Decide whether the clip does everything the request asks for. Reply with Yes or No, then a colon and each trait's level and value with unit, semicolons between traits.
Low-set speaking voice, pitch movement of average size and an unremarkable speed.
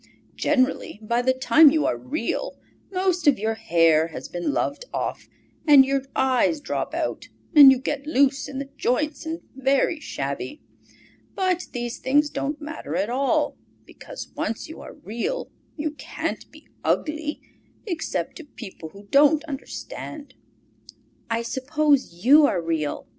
No: very high, 275 Hz; average, 4.9 semitones; average, 145 wpm